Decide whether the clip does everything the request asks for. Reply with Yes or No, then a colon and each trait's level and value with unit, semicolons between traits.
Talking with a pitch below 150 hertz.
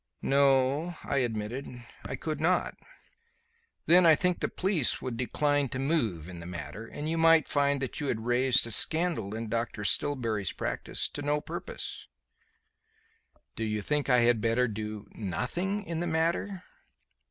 Yes: low, 135 Hz